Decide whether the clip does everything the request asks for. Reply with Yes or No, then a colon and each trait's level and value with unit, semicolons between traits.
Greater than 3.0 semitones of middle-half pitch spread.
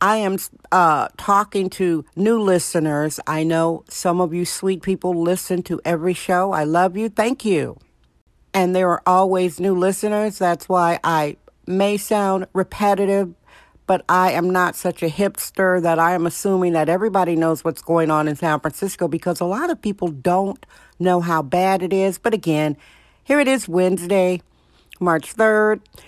No: narrow, 2.4 semitones